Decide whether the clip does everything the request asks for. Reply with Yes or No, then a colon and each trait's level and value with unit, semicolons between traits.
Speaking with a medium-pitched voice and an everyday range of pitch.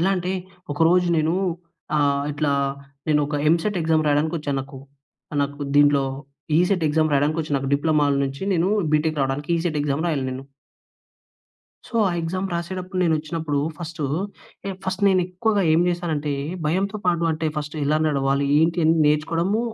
Yes: medium, 160 Hz; average, 3.1 semitones